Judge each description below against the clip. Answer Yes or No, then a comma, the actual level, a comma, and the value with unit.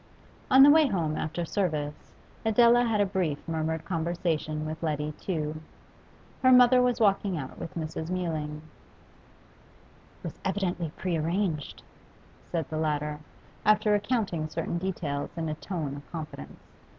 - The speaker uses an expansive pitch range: No, average, 4.7 semitones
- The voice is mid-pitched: Yes, medium, 165 Hz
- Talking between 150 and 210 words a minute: No, average, 140 wpm